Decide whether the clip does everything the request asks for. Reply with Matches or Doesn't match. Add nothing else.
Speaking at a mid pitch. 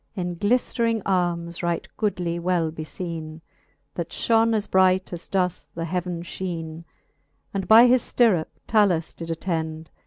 Matches